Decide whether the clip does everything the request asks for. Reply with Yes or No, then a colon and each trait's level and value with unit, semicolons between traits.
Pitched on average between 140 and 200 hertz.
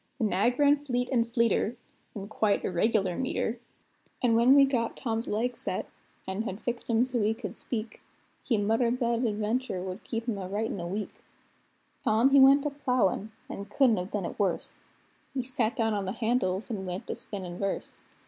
No: high, 225 Hz